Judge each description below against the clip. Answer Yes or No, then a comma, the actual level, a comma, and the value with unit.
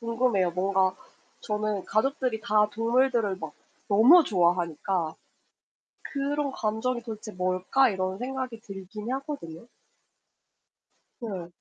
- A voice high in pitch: Yes, high, 215 Hz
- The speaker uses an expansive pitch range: No, average, 5.0 semitones